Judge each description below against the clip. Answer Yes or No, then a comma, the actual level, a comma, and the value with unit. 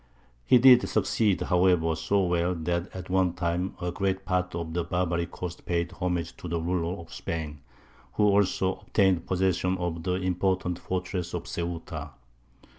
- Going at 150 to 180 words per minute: Yes, average, 160 wpm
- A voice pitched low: Yes, very low, 90 Hz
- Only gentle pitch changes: Yes, narrow, 1.7 semitones